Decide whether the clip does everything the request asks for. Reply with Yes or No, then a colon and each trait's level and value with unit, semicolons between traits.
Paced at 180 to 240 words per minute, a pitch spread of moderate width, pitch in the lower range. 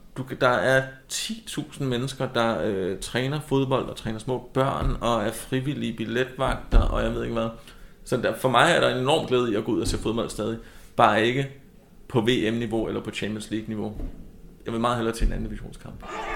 Yes: average, 195 wpm; average, 3.1 semitones; low, 120 Hz